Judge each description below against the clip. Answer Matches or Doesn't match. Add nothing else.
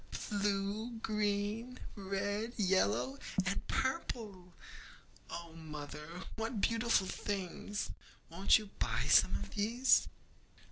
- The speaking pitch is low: Doesn't match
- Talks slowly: Matches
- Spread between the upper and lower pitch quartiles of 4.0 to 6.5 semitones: Doesn't match